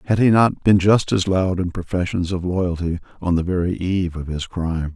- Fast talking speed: Yes, fast, 220 wpm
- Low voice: Yes, very low, 90 Hz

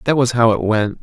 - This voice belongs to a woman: No, male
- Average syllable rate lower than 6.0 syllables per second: Yes, 5.5 syllables/s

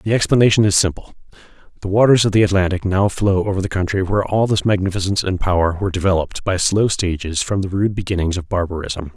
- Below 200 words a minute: No, fast, 205 wpm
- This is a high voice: No, very low, 95 Hz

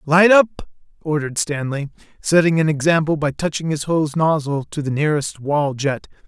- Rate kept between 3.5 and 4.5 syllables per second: No, 5.3 syllables/s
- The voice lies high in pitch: No, medium, 150 Hz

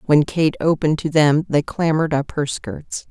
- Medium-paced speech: Yes, average, 195 wpm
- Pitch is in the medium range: Yes, medium, 150 Hz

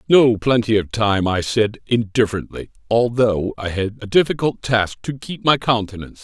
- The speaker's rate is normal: Yes, average, 165 wpm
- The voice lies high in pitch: No, low, 115 Hz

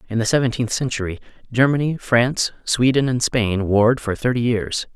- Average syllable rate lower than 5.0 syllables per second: No, 5.4 syllables/s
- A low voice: Yes, low, 120 Hz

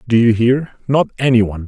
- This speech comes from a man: Yes, male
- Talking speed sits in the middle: No, fast, 215 wpm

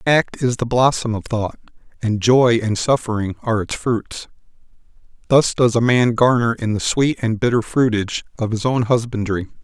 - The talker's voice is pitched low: Yes, low, 115 Hz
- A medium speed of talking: Yes, average, 175 wpm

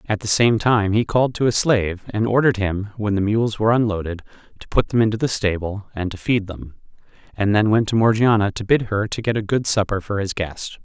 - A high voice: No, low, 105 Hz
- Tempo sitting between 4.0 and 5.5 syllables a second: No, 5.7 syllables/s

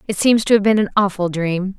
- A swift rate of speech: Yes, fast, 270 wpm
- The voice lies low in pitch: No, high, 195 Hz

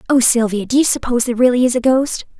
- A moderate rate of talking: No, fast, 250 wpm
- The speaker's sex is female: Yes, female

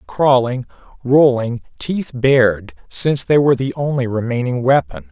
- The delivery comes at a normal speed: No, slow, 130 wpm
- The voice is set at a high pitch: No, low, 125 Hz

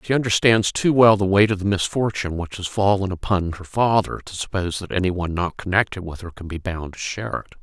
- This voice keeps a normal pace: No, fast, 235 wpm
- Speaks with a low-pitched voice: Yes, very low, 95 Hz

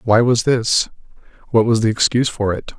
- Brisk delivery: No, average, 195 wpm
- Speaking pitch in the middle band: No, low, 115 Hz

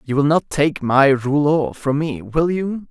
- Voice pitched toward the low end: No, medium, 145 Hz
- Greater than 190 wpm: Yes, fast, 205 wpm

